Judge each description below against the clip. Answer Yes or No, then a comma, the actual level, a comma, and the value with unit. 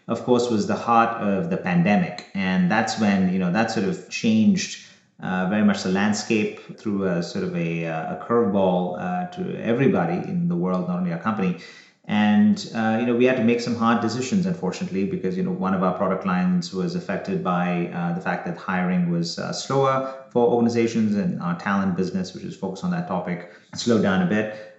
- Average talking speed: No, fast, 210 wpm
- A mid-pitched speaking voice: No, low, 130 Hz